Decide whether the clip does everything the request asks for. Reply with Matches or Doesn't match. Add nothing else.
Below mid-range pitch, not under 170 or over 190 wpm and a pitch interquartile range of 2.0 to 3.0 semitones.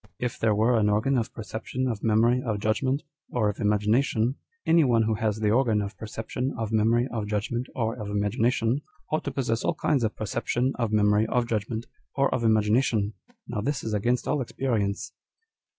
Matches